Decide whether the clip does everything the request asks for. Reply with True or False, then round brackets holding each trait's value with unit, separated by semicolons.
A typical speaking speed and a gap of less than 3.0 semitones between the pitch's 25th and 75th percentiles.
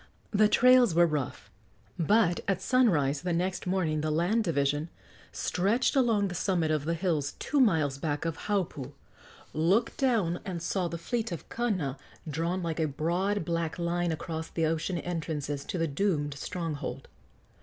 False (160 wpm; 3.9 semitones)